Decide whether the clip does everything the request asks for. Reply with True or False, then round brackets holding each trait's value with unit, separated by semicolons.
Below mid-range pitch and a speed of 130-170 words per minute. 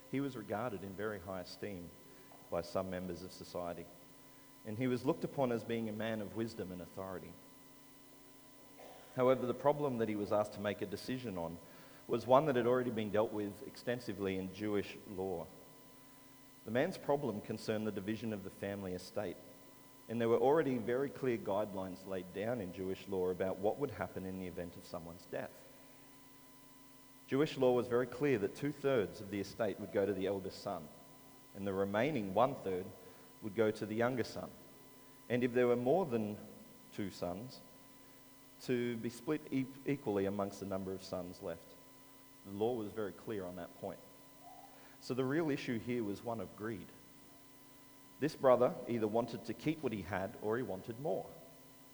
False (110 Hz; 180 wpm)